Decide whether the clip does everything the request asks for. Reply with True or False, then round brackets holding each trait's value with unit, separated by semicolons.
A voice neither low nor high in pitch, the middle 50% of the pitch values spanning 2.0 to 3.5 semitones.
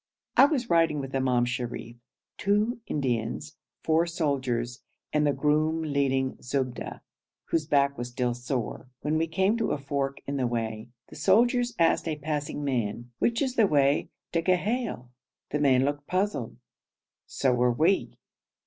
False (145 Hz; 4.8 semitones)